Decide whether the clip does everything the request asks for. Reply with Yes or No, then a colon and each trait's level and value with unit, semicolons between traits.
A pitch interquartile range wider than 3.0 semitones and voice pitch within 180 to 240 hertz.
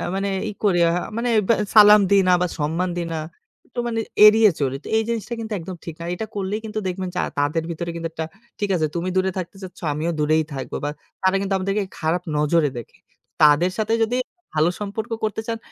Yes: average, 4.4 semitones; medium, 185 Hz